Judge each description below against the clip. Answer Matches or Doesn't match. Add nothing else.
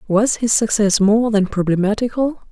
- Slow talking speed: Doesn't match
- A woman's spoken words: Matches